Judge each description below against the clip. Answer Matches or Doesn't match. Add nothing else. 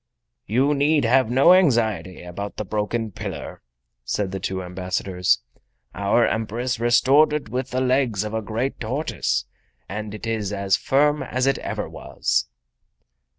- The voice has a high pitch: Doesn't match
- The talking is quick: Doesn't match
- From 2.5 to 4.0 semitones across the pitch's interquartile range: Doesn't match